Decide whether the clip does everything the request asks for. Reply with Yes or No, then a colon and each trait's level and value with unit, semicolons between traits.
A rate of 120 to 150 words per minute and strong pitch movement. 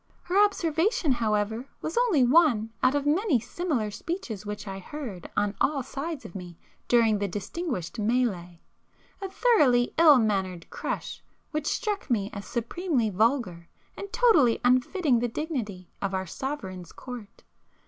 Yes: average, 140 wpm; wide, 7.1 semitones